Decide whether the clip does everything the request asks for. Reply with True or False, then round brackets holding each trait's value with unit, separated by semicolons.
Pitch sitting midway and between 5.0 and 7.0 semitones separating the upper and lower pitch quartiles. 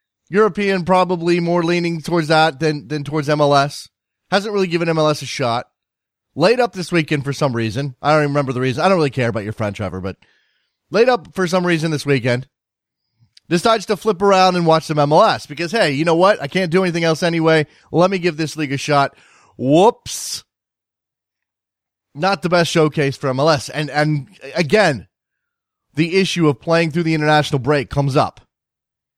False (155 Hz; 3.8 semitones)